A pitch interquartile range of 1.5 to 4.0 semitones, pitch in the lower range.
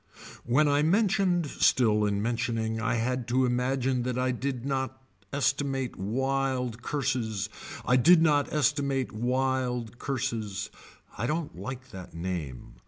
Yes: average, 3.0 semitones; low, 130 Hz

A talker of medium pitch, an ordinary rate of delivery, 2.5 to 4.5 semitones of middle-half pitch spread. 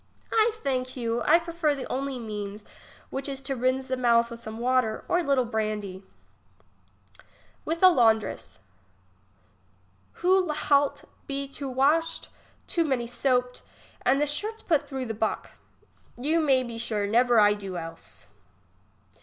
No: very high, 255 Hz; average, 145 wpm; average, 4.0 semitones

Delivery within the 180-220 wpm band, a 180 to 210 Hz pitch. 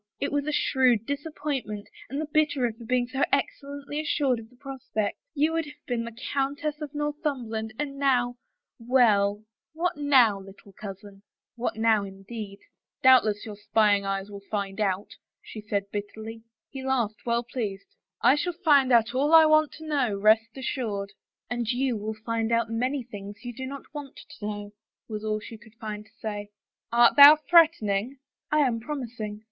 No: average, 185 wpm; high, 235 Hz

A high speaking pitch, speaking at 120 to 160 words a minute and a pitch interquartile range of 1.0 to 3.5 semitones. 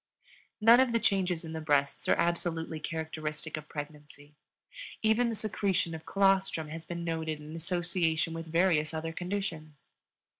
No: medium, 165 Hz; average, 150 wpm; average, 2.9 semitones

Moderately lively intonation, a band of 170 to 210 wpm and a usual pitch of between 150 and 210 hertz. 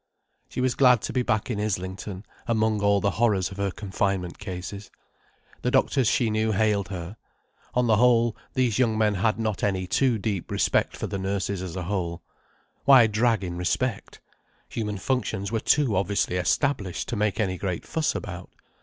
No: average, 3.2 semitones; average, 180 wpm; low, 105 Hz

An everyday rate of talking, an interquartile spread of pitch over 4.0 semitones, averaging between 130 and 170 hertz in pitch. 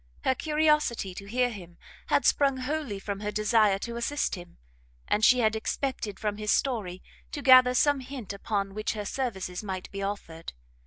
No: average, 175 wpm; average, 4.5 semitones; high, 215 Hz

